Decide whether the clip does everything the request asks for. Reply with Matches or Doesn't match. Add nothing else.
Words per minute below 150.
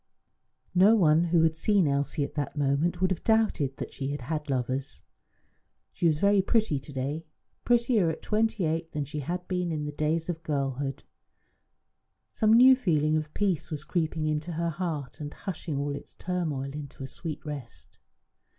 Doesn't match